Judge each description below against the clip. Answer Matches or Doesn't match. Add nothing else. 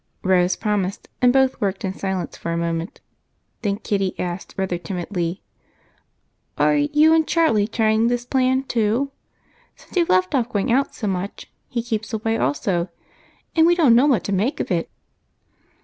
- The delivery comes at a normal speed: Matches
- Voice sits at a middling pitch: Doesn't match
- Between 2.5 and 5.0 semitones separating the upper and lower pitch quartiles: Doesn't match